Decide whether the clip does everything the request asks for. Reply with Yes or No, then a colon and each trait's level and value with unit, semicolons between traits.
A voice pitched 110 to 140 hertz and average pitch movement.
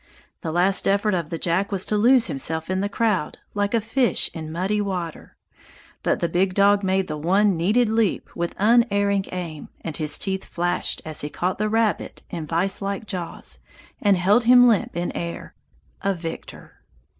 No: high, 190 Hz; average, 3.4 semitones